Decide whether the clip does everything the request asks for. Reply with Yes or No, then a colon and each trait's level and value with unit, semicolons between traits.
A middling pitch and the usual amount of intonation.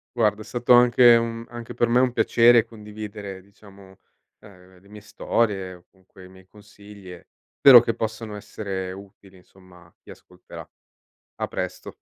No: low, 105 Hz; average, 3.5 semitones